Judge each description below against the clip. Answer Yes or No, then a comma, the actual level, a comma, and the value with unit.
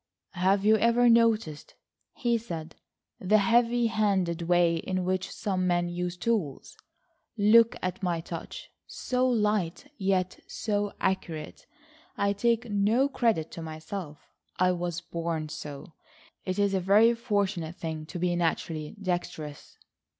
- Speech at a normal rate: No, slow, 130 wpm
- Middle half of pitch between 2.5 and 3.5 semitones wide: No, average, 4.1 semitones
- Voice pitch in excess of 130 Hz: Yes, medium, 185 Hz